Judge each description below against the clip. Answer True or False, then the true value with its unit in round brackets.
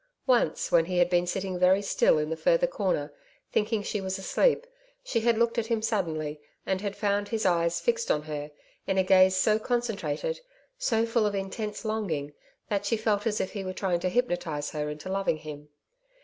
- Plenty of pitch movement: False (4.3 semitones)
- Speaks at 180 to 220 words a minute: True (200 wpm)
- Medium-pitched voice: False (195 Hz)